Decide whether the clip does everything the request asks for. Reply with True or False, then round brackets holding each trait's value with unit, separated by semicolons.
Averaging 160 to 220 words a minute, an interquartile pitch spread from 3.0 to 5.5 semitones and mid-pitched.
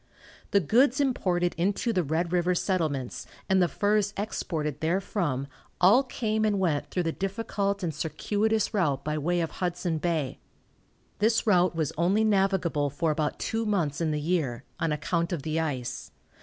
True (165 wpm; 4.4 semitones; 175 Hz)